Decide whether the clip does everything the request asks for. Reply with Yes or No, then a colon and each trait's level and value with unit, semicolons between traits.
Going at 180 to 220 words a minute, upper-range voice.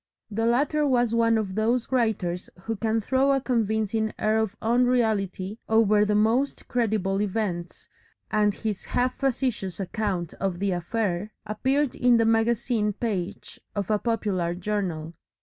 No: average, 145 wpm; high, 220 Hz